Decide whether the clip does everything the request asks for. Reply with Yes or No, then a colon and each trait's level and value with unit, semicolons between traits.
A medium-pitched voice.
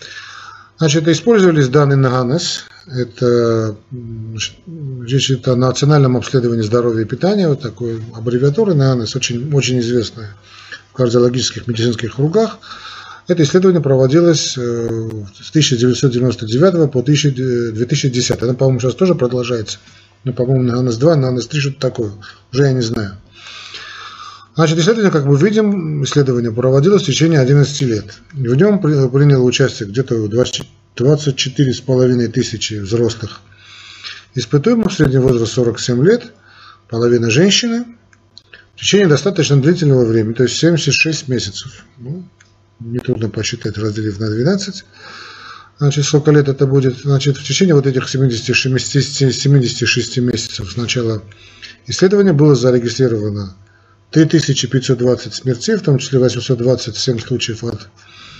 No: low, 130 Hz